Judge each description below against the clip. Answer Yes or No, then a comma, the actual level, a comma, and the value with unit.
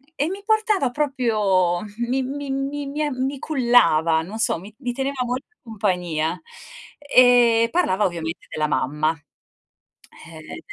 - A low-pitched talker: No, high, 235 Hz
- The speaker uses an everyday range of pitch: No, wide, 8.0 semitones